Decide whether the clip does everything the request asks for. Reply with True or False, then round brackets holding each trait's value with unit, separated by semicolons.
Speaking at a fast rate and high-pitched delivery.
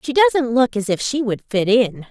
True (255 wpm; 240 Hz)